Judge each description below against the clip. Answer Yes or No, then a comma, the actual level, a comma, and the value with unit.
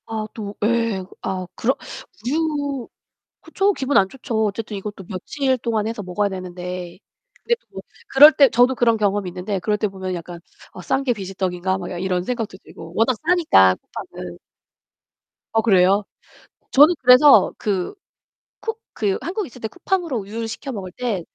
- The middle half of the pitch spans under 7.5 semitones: Yes, wide, 5.6 semitones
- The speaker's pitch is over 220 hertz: No, high, 215 Hz